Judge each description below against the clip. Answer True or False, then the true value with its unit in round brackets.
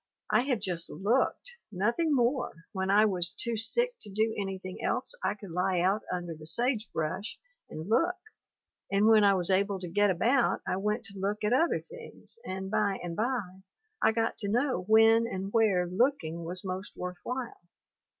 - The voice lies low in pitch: False (205 Hz)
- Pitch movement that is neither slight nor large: True (3.8 semitones)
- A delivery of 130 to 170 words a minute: False (190 wpm)